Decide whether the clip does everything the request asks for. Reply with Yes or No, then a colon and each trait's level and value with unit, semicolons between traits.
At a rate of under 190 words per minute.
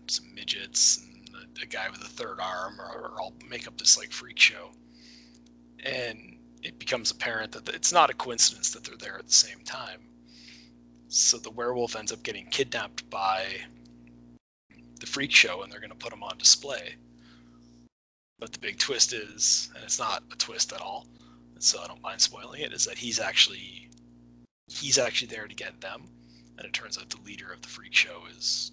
No: average, 200 wpm